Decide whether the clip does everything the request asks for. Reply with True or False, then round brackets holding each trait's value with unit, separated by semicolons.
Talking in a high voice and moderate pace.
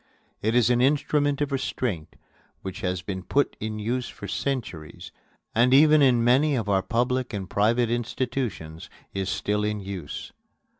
False (115 Hz; 150 wpm)